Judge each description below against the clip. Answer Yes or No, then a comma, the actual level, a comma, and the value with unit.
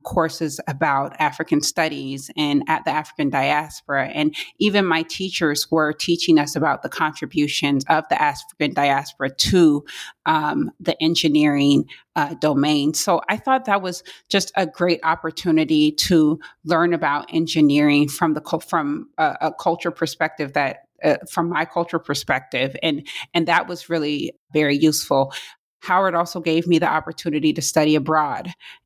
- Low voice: No, medium, 160 Hz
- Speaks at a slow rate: No, average, 150 wpm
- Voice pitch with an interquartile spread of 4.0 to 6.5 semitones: No, narrow, 2.4 semitones